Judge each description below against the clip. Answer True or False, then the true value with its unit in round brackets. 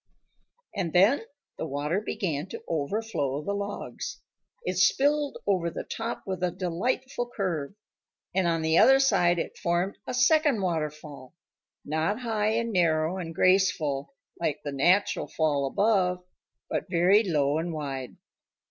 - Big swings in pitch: False (4.7 semitones)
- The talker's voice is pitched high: False (180 Hz)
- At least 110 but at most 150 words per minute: True (140 wpm)